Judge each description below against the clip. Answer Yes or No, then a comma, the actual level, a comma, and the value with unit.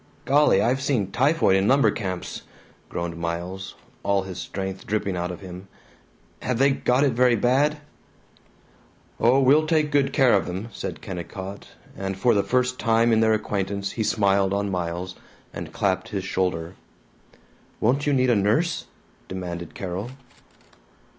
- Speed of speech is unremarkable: Yes, average, 155 wpm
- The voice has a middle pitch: No, low, 100 Hz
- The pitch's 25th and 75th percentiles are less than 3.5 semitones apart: No, average, 5.2 semitones